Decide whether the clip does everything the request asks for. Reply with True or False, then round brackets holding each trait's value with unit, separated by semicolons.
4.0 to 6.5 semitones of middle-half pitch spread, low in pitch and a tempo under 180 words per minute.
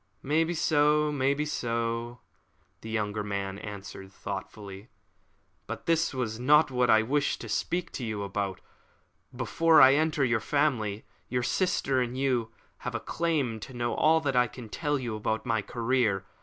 True (5.1 semitones; 125 Hz; 160 wpm)